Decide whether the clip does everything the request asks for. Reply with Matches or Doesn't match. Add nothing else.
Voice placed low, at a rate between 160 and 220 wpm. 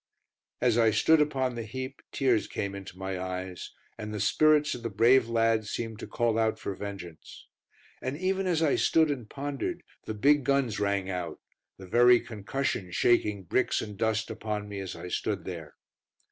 Matches